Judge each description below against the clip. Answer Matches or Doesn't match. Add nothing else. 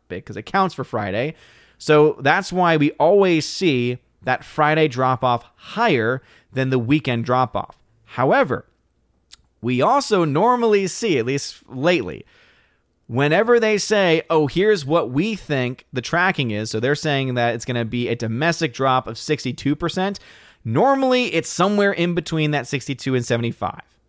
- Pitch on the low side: Doesn't match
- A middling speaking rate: Matches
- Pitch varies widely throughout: Matches